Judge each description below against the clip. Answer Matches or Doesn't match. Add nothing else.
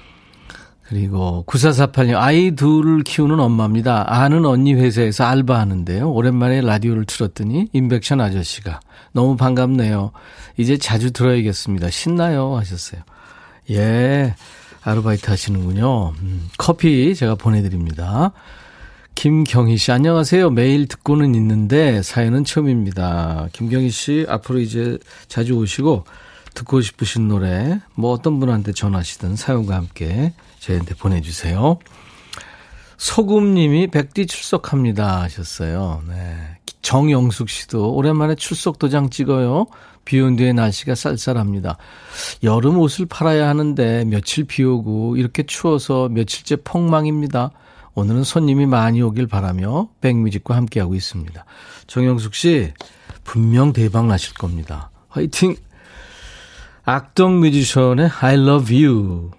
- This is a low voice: Matches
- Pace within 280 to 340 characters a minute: Matches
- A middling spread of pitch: Doesn't match